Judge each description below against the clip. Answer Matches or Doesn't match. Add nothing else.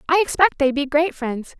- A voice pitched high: Matches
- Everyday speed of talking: Doesn't match